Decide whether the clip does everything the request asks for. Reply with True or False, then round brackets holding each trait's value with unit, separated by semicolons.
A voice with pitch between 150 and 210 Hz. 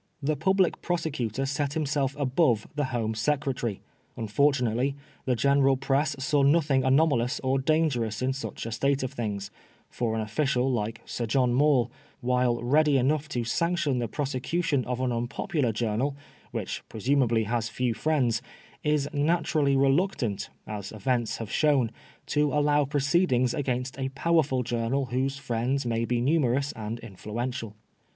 False (130 Hz)